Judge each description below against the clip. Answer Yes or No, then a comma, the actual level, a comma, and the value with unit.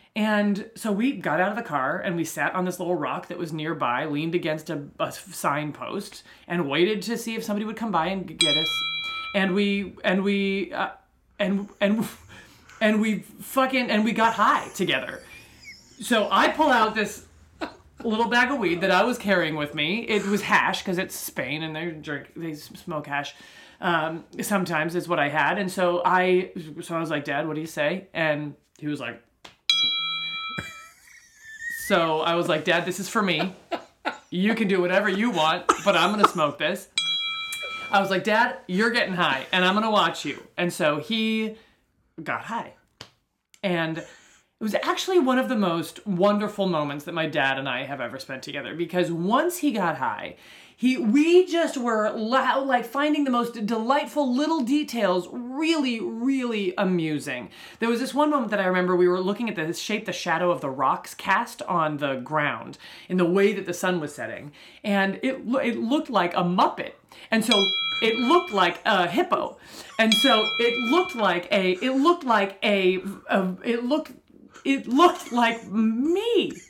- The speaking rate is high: No, average, 185 wpm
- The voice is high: Yes, high, 205 Hz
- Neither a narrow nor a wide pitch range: No, wide, 6.2 semitones